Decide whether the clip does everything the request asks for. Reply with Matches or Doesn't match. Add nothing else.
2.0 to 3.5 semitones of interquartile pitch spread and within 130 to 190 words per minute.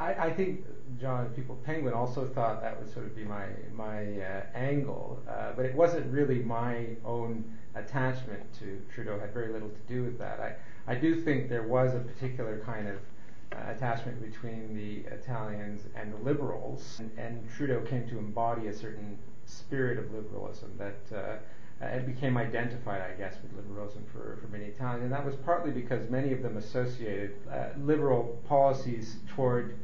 Matches